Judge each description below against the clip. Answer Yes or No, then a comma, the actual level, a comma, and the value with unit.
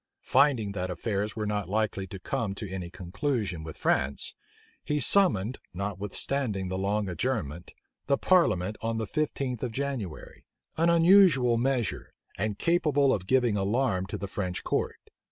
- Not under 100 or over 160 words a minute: Yes, average, 150 wpm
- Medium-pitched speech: No, low, 105 Hz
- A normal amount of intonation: No, wide, 5.9 semitones